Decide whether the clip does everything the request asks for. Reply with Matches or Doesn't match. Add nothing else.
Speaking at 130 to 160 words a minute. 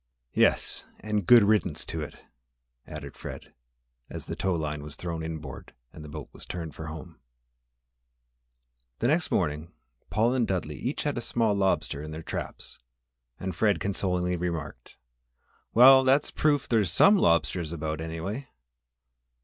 Matches